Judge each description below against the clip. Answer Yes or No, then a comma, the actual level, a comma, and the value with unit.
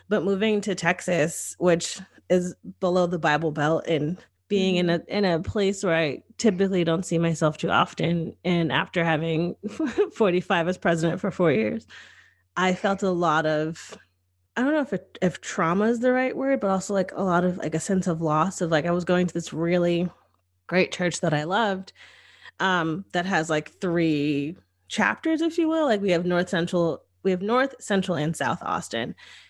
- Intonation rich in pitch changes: No, average, 3.1 semitones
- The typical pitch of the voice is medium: Yes, medium, 175 Hz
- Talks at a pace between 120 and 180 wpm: No, average, 195 wpm